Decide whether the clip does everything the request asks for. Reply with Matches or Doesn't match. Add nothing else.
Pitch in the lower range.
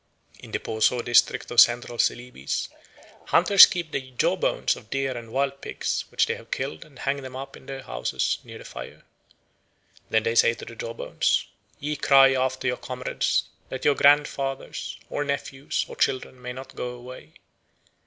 Matches